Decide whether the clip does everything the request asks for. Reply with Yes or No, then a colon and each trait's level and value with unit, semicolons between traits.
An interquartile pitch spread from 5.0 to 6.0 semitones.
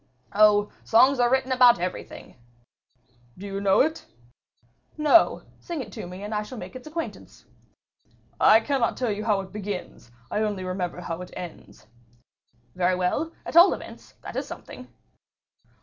Yes: wide, 5.6 semitones